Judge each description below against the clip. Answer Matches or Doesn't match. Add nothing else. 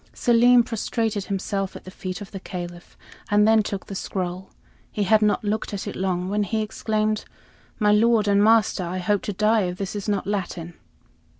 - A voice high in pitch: Matches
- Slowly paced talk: Doesn't match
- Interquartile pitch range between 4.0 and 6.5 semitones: Doesn't match